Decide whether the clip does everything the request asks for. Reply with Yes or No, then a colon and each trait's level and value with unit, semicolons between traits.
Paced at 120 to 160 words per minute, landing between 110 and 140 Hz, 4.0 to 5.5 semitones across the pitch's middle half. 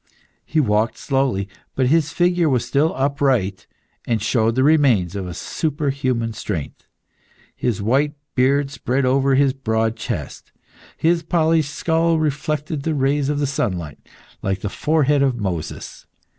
Yes: average, 140 wpm; low, 135 Hz; average, 4.8 semitones